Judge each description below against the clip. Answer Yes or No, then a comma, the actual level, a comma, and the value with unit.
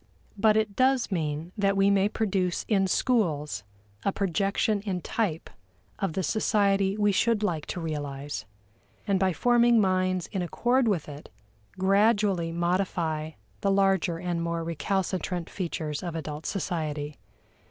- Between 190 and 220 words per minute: No, average, 140 wpm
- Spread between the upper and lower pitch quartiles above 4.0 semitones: No, average, 3.6 semitones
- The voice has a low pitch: No, high, 190 Hz